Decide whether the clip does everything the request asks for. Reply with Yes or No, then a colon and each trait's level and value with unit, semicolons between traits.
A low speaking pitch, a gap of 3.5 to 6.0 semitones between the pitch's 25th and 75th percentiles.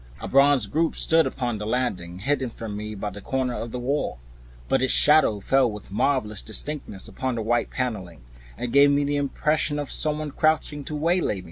Yes: low, 130 Hz; average, 5.3 semitones